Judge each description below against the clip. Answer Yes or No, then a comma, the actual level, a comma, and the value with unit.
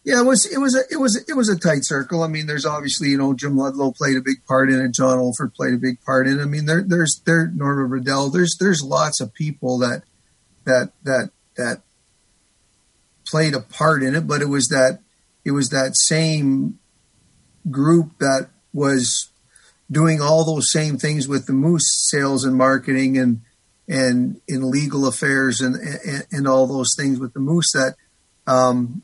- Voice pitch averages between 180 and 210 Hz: No, medium, 140 Hz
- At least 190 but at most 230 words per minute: Yes, average, 195 wpm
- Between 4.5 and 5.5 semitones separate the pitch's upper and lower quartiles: No, average, 3.1 semitones